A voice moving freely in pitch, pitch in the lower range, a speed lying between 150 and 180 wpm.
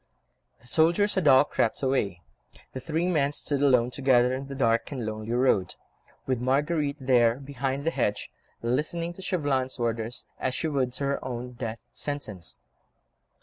No: average, 3.3 semitones; low, 130 Hz; average, 160 wpm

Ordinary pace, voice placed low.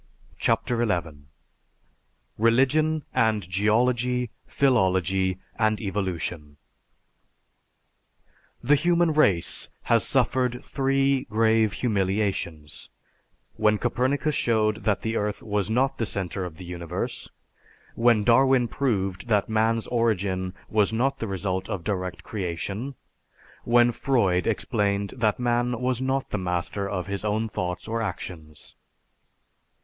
No: slow, 115 wpm; low, 110 Hz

